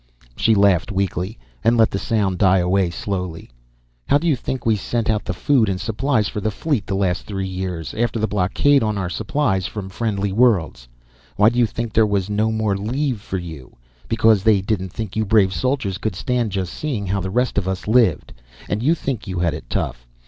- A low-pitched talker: Yes, low, 105 Hz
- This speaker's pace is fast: Yes, fast, 215 wpm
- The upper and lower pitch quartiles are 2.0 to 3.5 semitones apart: Yes, average, 3.2 semitones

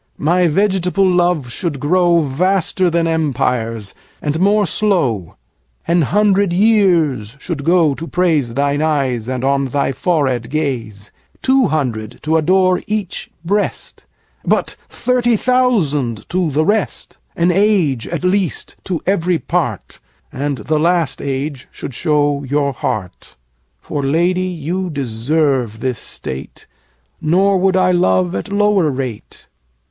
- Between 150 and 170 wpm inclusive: No, slow, 135 wpm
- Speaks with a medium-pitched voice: Yes, medium, 155 Hz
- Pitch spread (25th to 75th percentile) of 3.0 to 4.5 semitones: No, wide, 5.5 semitones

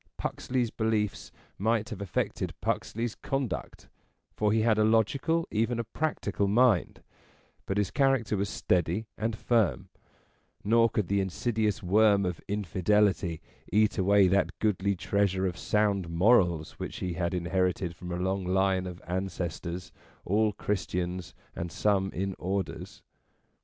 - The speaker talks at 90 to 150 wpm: Yes, slow, 135 wpm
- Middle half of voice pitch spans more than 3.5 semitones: No, average, 3.1 semitones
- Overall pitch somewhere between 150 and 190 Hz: No, low, 100 Hz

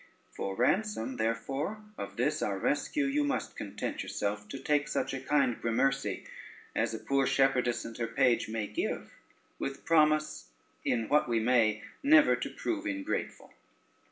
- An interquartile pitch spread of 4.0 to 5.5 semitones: Yes, average, 5.0 semitones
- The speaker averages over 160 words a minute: No, average, 155 wpm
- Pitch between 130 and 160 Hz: Yes, low, 135 Hz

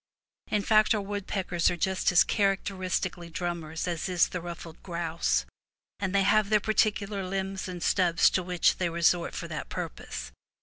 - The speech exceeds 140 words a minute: Yes, average, 170 wpm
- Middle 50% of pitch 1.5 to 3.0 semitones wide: Yes, narrow, 2.5 semitones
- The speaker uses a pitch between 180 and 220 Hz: Yes, medium, 185 Hz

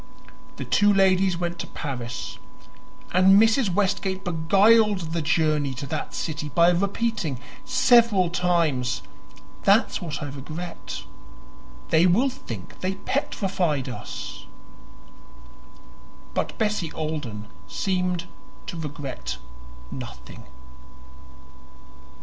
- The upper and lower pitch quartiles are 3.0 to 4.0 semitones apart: No, average, 4.7 semitones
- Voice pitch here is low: No, medium, 175 Hz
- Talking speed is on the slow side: Yes, slow, 95 wpm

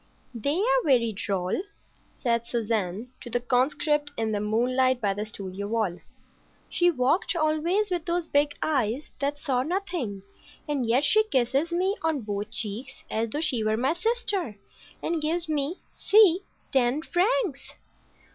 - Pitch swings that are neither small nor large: No, wide, 6.8 semitones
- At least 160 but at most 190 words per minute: No, average, 145 wpm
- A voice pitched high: Yes, very high, 270 Hz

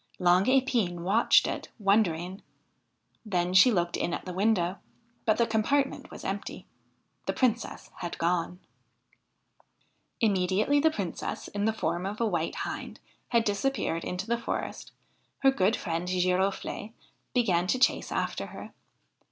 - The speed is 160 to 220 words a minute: No, average, 140 wpm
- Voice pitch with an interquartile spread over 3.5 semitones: Yes, average, 4.3 semitones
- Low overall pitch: No, high, 195 Hz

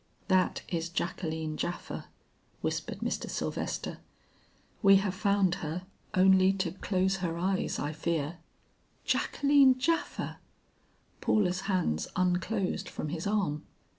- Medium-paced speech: No, slow, 110 wpm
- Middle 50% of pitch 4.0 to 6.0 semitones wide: No, narrow, 2.6 semitones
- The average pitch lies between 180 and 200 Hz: Yes, medium, 185 Hz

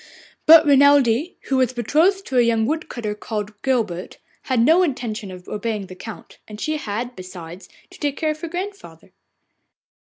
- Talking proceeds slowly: No, average, 175 wpm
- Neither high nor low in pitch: No, high, 245 Hz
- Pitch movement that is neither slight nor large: No, wide, 6.5 semitones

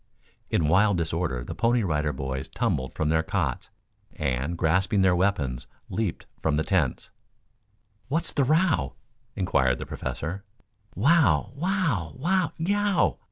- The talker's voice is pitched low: Yes, very low, 90 Hz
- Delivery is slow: Yes, slow, 130 wpm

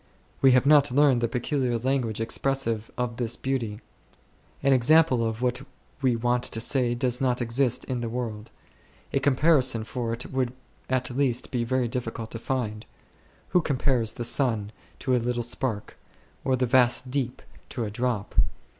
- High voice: No, low, 125 Hz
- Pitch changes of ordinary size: No, narrow, 2.2 semitones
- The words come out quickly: No, average, 165 wpm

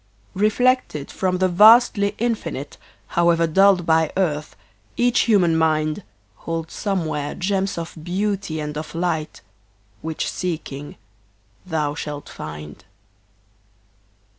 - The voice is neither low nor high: Yes, medium, 170 Hz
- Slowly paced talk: Yes, slow, 105 wpm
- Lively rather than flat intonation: No, average, 4.3 semitones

